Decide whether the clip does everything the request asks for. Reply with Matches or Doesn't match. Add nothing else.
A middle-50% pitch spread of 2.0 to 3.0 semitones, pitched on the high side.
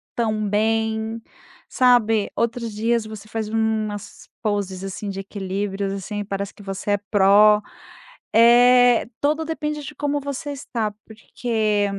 Matches